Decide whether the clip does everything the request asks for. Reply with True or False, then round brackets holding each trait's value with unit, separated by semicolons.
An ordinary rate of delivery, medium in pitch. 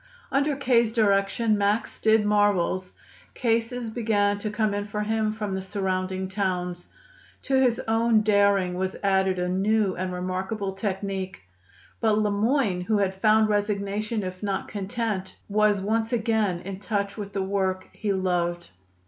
False (150 wpm; 205 Hz)